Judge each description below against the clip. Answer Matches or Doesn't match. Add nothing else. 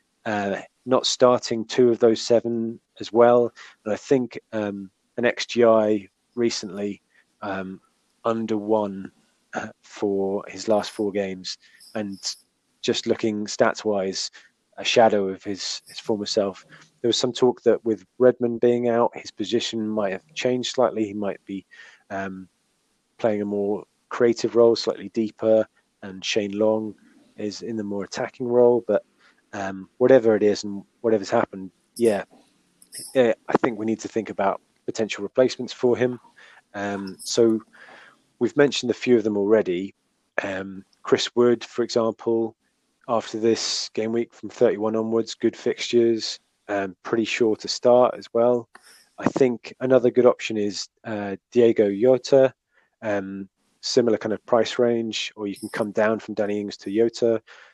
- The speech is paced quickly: Doesn't match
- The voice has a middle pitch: Doesn't match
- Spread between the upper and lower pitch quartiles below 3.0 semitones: Matches